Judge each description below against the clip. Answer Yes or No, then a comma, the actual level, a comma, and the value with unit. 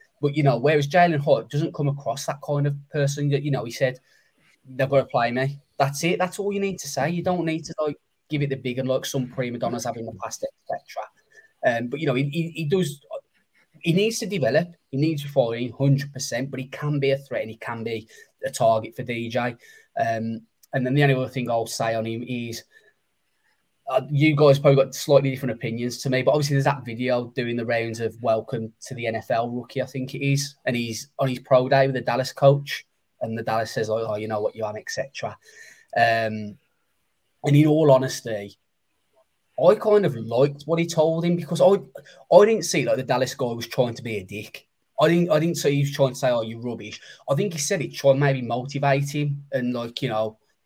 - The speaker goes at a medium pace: No, fast, 230 wpm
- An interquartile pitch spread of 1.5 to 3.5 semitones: No, average, 4.2 semitones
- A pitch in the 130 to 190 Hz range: Yes, low, 135 Hz